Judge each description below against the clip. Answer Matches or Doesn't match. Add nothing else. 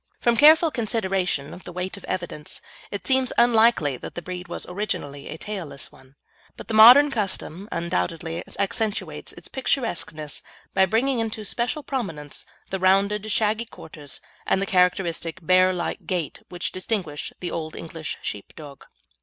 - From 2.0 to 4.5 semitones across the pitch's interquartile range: Doesn't match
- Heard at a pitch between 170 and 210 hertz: Matches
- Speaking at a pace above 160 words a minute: Doesn't match